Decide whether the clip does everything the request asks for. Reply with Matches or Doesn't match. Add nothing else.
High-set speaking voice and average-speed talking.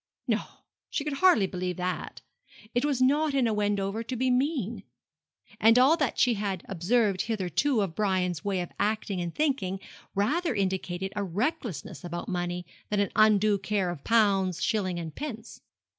Matches